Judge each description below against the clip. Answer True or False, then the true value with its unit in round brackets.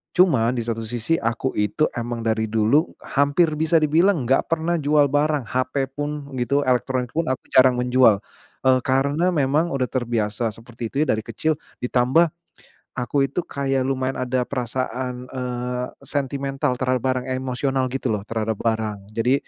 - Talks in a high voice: False (130 Hz)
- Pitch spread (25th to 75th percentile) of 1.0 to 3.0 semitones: True (2.7 semitones)